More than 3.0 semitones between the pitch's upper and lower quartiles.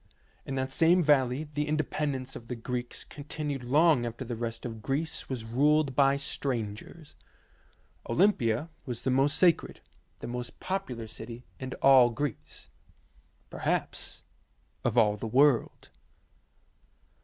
Yes: average, 3.8 semitones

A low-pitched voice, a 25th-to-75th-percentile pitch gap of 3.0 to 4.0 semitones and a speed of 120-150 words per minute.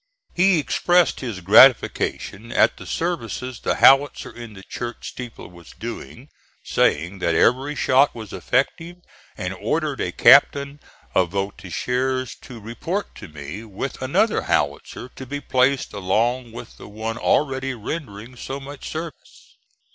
No: low, 125 Hz; average, 4.9 semitones; average, 140 wpm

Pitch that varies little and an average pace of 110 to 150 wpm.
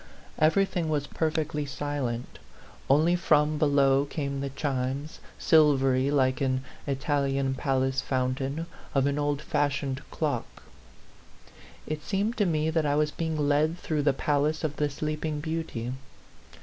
Yes: narrow, 2.2 semitones; average, 140 wpm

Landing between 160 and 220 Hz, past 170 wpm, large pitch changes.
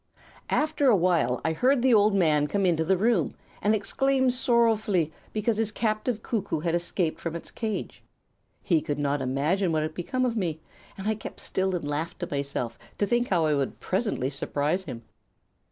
Yes: medium, 185 Hz; average, 185 wpm; wide, 5.9 semitones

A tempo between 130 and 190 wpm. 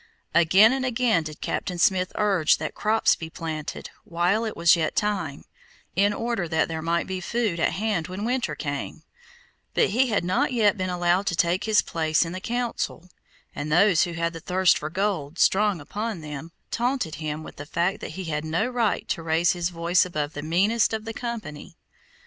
No: average, 200 wpm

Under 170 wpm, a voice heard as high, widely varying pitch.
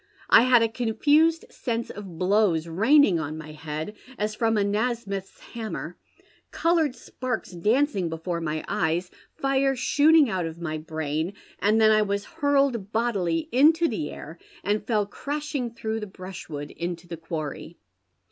Yes: average, 145 wpm; high, 210 Hz; wide, 6.8 semitones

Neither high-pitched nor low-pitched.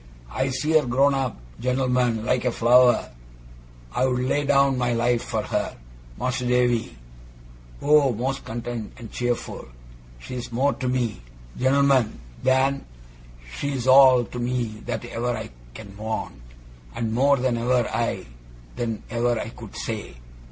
No: low, 125 Hz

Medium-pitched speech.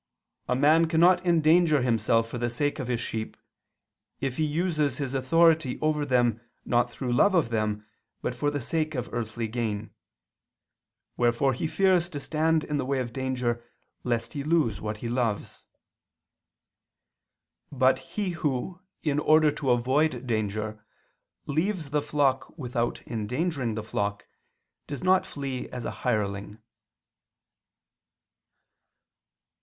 No: low, 130 Hz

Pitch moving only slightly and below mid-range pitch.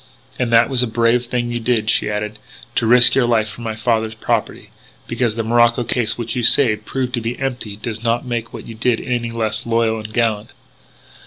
Yes: narrow, 1.5 semitones; low, 115 Hz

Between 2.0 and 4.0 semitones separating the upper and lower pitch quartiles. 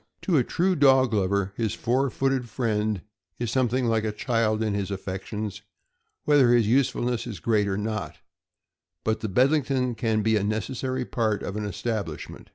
Yes: average, 3.3 semitones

